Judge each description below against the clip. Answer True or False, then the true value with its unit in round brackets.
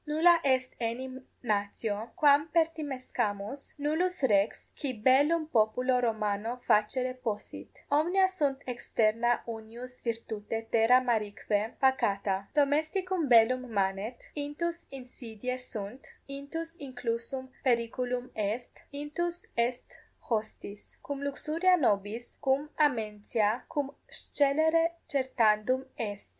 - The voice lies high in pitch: True (255 Hz)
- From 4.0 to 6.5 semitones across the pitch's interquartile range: True (4.5 semitones)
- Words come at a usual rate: False (100 wpm)